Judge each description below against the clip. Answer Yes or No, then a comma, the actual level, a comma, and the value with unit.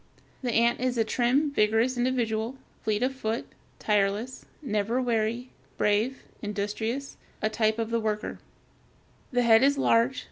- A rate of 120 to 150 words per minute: Yes, average, 140 wpm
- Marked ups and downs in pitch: No, average, 2.7 semitones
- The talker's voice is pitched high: Yes, high, 230 Hz